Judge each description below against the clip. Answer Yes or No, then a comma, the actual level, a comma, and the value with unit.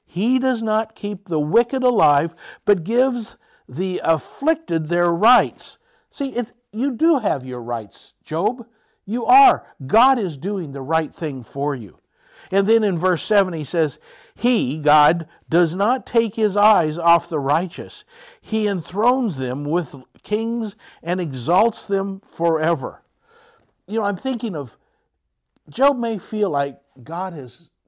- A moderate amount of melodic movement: No, wide, 6.4 semitones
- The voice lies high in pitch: Yes, high, 195 Hz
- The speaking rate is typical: Yes, average, 145 wpm